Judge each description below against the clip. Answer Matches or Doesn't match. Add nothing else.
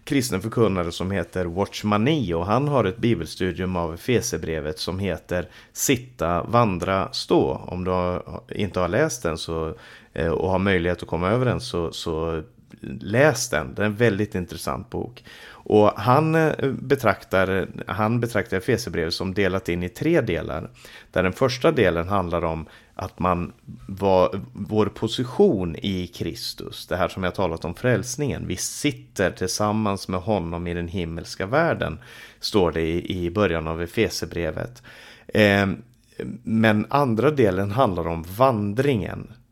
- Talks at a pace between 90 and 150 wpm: Matches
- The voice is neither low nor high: Doesn't match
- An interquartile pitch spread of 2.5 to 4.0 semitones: Doesn't match